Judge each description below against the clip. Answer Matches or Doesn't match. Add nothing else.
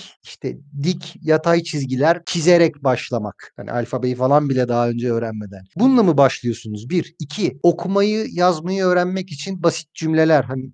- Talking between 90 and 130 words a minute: Doesn't match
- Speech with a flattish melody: Doesn't match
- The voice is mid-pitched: Matches